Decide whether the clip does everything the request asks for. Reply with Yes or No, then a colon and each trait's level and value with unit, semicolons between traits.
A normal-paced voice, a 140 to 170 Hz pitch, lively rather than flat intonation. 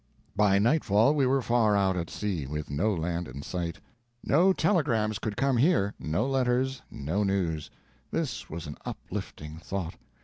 No: average, 160 wpm; low, 100 Hz; wide, 7.0 semitones